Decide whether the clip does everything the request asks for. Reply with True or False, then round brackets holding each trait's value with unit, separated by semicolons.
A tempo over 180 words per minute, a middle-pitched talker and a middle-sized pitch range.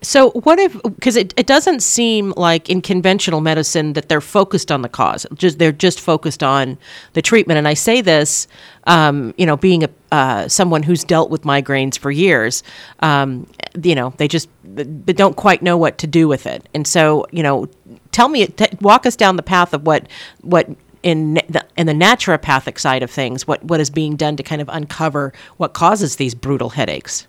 True (205 wpm; 160 Hz; 4.1 semitones)